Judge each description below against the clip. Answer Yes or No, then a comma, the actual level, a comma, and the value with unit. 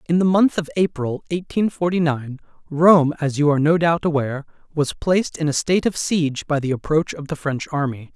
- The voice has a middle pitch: Yes, medium, 155 Hz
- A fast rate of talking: Yes, fast, 215 wpm